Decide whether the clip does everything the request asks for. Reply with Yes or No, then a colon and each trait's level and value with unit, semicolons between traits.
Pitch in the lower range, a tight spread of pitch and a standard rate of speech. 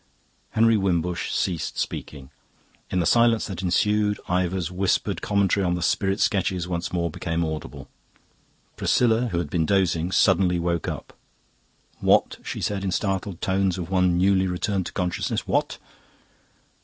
Yes: very low, 90 Hz; narrow, 2.3 semitones; average, 150 wpm